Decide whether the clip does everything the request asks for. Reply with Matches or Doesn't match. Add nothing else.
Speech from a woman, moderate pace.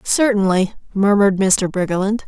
Doesn't match